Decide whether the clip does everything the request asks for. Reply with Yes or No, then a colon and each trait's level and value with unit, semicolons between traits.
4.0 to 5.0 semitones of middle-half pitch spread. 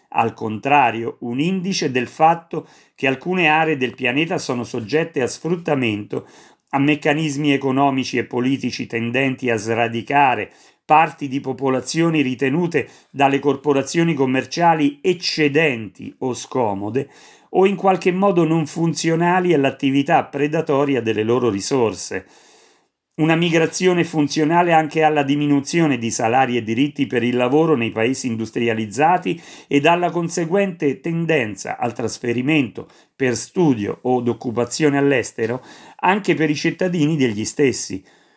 Yes: average, 4.7 semitones